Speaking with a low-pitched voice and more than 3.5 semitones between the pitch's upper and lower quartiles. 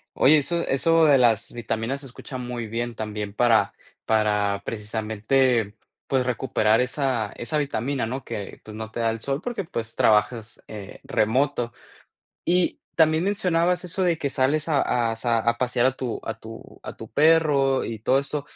Yes: low, 125 Hz; average, 4.4 semitones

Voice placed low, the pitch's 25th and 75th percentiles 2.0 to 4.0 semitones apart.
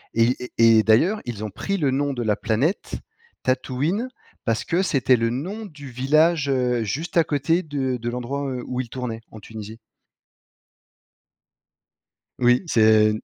No: low, 130 Hz; average, 4.5 semitones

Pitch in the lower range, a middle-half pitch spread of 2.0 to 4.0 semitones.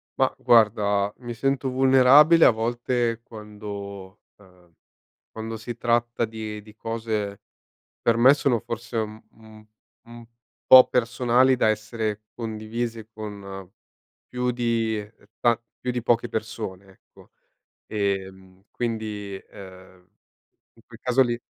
Yes: low, 110 Hz; narrow, 2.5 semitones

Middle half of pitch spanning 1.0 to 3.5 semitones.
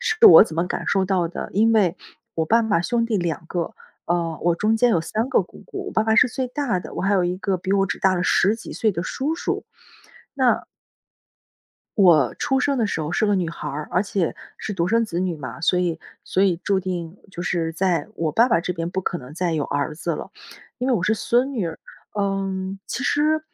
No: average, 4.7 semitones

